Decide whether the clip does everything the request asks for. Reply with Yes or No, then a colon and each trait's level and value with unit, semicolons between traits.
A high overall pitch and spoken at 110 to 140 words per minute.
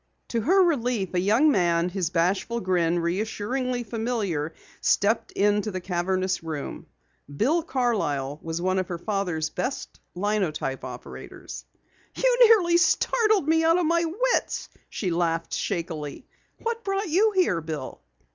Yes: high, 205 Hz; slow, 135 wpm